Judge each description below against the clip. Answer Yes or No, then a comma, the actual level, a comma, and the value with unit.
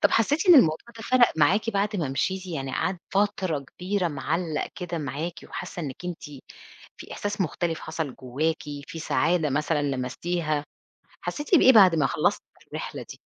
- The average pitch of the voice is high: No, medium, 170 Hz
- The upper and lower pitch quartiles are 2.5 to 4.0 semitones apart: No, average, 4.7 semitones